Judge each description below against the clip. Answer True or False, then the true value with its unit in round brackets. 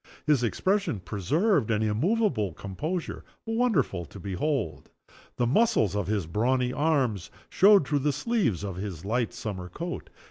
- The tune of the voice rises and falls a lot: True (8.5 semitones)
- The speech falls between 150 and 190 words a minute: False (140 wpm)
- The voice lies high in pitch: False (120 Hz)